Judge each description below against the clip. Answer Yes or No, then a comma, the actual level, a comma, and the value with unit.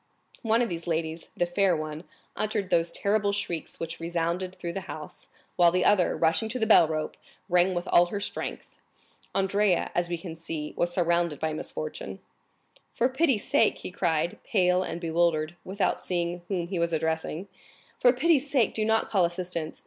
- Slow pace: No, average, 175 wpm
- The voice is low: No, medium, 175 Hz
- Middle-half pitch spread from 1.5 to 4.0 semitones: Yes, average, 3.2 semitones